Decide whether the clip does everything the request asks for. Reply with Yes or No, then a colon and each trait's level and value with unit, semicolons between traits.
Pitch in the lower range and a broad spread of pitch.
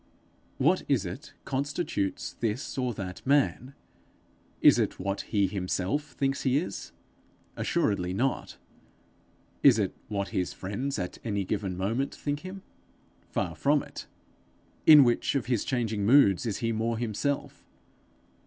Yes: low, 115 Hz; wide, 5.8 semitones